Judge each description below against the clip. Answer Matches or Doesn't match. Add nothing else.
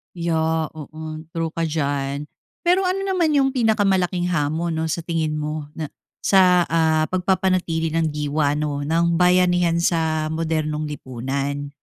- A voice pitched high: Doesn't match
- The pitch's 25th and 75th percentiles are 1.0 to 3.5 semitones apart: Matches